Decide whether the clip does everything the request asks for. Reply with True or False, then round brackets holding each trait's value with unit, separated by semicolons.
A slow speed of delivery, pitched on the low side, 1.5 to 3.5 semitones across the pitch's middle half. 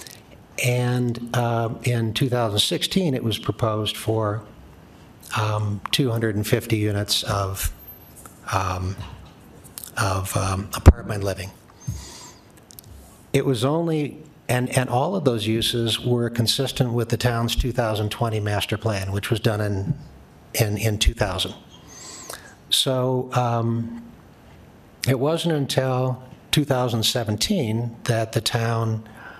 True (100 wpm; 115 Hz; 3.1 semitones)